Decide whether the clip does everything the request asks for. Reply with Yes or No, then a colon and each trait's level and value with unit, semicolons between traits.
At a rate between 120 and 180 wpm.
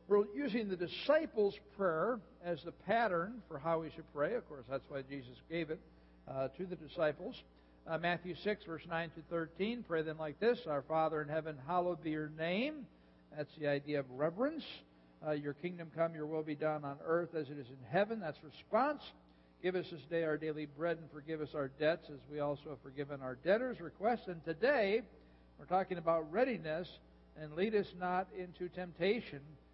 No: average, 195 wpm